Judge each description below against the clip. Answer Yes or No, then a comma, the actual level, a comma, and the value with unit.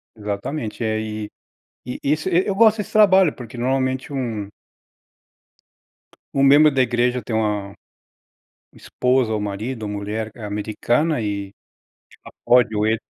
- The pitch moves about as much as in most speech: Yes, average, 4.4 semitones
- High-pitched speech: No, low, 120 Hz